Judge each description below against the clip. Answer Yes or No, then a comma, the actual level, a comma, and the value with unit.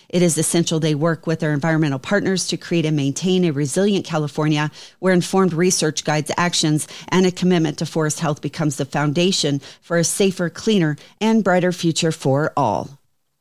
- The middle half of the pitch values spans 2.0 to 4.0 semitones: Yes, average, 3.0 semitones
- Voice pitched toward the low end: No, medium, 165 Hz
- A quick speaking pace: No, average, 175 wpm